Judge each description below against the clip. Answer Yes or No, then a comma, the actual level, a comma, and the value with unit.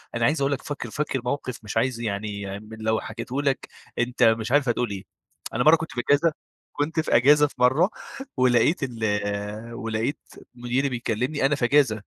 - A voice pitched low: Yes, low, 125 Hz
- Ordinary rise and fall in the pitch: Yes, average, 4.1 semitones